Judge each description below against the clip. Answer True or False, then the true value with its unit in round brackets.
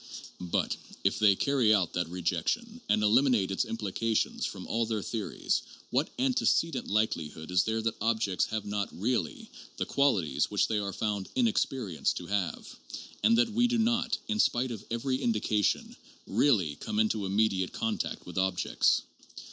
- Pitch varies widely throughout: True (5.7 semitones)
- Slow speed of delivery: False (165 wpm)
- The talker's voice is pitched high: False (110 Hz)